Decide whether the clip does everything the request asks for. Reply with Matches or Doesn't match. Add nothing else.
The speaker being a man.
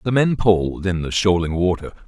Matches